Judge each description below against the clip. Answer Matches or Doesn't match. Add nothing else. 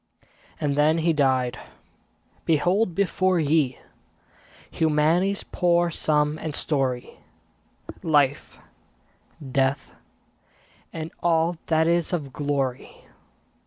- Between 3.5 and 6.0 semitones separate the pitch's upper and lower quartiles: Doesn't match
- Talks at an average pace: Doesn't match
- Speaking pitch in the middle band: Matches